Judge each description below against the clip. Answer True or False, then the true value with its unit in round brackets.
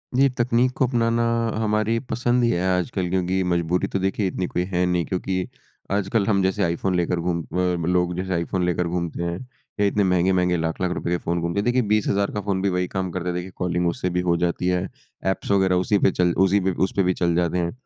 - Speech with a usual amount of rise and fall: False (2.2 semitones)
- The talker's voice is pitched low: True (90 Hz)